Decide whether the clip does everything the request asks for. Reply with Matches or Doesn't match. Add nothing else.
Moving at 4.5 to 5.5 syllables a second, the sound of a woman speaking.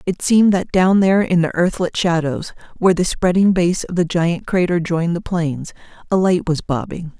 Matches